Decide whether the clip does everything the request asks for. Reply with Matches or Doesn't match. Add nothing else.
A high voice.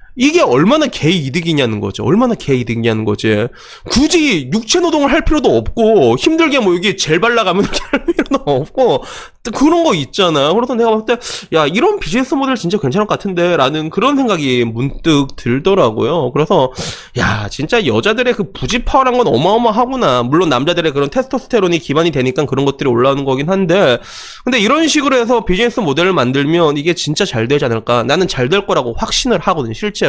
Matches